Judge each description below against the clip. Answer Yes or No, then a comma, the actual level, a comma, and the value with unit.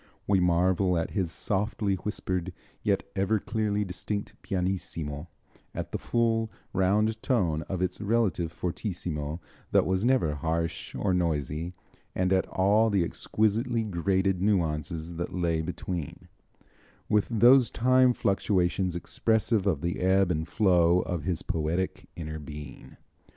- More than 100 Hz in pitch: No, very low, 95 Hz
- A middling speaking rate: No, slow, 130 wpm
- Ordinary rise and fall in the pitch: Yes, average, 3.7 semitones